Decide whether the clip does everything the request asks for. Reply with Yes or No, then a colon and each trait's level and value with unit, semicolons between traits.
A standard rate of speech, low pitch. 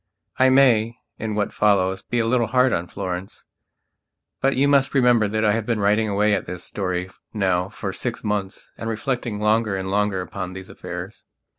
Yes: average, 185 wpm; low, 105 Hz